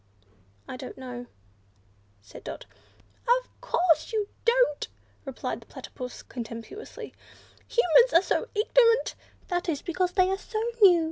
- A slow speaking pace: Yes, slow, 125 wpm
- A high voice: Yes, very high, 360 Hz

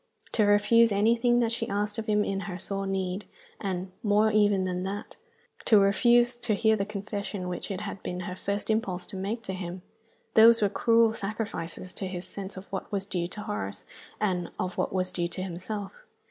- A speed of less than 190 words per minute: No, average, 200 wpm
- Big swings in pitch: No, narrow, 2.6 semitones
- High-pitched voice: Yes, high, 200 Hz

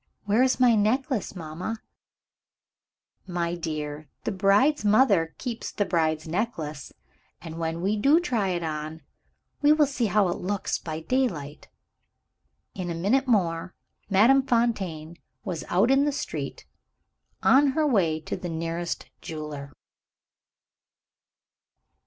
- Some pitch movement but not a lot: No, wide, 6.6 semitones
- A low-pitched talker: No, high, 190 Hz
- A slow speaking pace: Yes, slow, 130 wpm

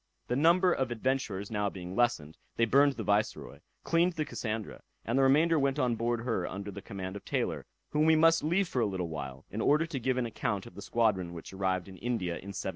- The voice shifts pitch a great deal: Yes, wide, 6.4 semitones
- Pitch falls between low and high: No, low, 115 Hz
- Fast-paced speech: Yes, fast, 230 wpm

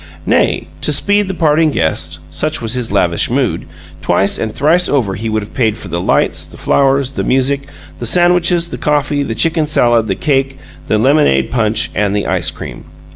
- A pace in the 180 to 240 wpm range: Yes, average, 190 wpm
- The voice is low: Yes, low, 130 Hz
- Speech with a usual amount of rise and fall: No, wide, 5.9 semitones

